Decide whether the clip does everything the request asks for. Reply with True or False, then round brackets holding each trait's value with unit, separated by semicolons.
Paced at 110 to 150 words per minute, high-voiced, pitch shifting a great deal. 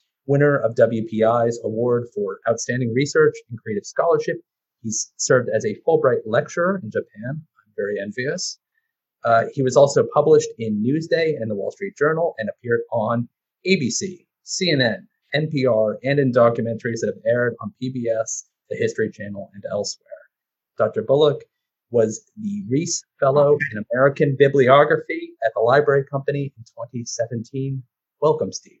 False (145 wpm; 140 Hz; 8.4 semitones)